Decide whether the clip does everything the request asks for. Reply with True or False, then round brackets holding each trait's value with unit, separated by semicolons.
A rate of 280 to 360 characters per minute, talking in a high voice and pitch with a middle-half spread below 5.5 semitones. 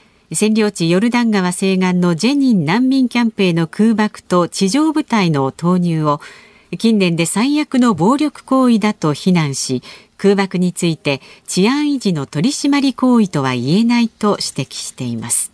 False (315 characters per minute; 195 Hz; 5.9 semitones)